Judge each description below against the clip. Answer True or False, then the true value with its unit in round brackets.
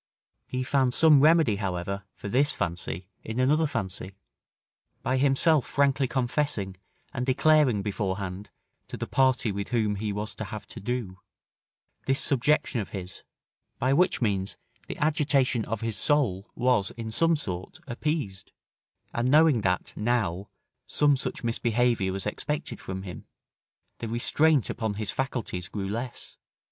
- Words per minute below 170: True (145 wpm)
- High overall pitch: False (120 Hz)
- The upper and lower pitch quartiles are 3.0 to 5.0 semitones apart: False (5.5 semitones)